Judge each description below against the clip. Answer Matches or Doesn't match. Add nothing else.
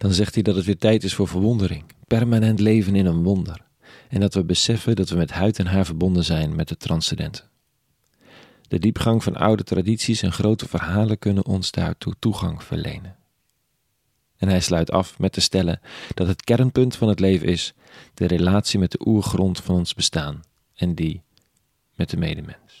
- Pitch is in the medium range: Doesn't match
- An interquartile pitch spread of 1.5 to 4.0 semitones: Matches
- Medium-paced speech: Matches